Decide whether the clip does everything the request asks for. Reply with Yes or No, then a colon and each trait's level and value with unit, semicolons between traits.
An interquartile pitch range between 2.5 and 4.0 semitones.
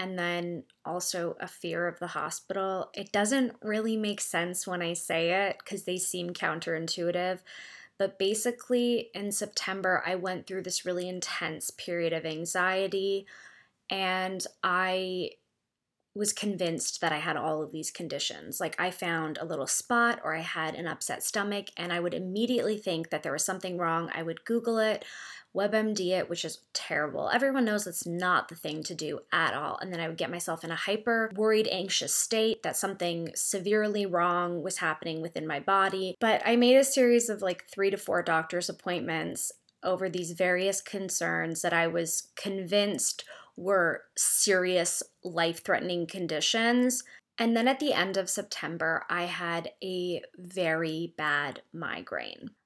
Yes: average, 3.1 semitones